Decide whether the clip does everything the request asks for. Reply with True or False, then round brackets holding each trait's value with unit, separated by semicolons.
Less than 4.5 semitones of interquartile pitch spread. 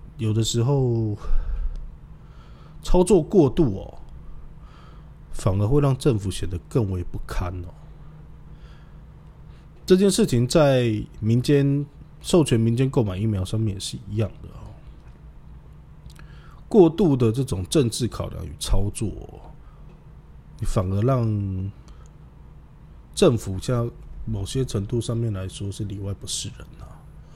False (5.3 semitones)